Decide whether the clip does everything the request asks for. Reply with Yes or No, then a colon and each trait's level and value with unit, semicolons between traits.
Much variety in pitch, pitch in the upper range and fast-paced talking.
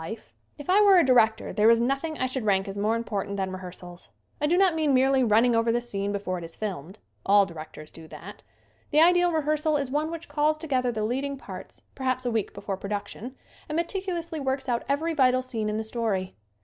Yes: wide, 6.6 semitones; high, 245 Hz; fast, 225 wpm